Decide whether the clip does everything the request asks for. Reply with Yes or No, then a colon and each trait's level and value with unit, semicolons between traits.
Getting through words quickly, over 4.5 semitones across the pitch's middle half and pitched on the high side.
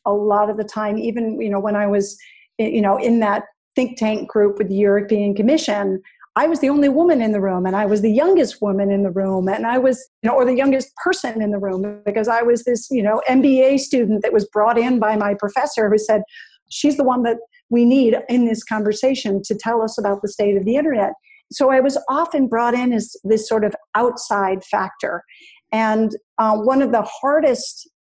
No: fast, 225 wpm; average, 4.0 semitones; high, 225 Hz